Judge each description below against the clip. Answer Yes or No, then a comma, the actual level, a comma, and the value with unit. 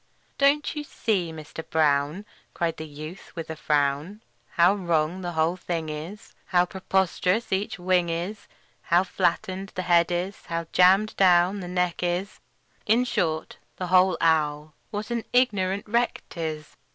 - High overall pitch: No, medium, 180 Hz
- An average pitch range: Yes, average, 3.2 semitones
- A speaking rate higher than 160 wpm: No, average, 155 wpm